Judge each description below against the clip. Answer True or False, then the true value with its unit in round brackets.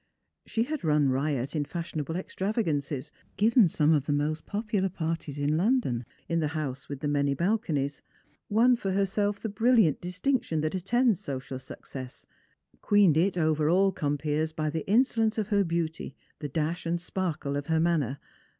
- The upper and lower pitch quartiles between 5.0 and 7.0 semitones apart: True (5.4 semitones)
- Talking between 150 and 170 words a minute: True (165 wpm)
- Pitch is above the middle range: False (165 Hz)